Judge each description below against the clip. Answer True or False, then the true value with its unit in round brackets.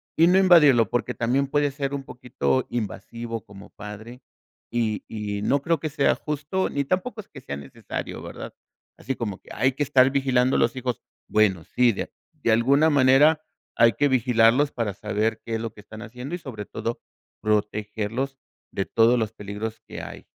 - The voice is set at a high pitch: False (125 Hz)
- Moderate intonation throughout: True (4.3 semitones)